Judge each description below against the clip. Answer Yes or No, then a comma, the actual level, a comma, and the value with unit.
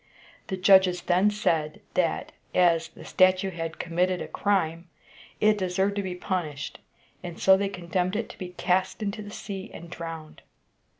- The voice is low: No, medium, 185 Hz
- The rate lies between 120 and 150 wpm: No, average, 165 wpm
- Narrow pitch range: Yes, narrow, 2.3 semitones